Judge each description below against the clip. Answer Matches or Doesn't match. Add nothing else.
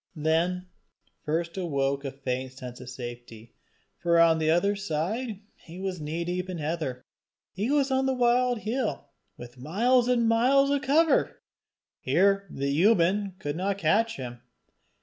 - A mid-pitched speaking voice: Matches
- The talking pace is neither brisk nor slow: Matches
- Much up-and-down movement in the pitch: Matches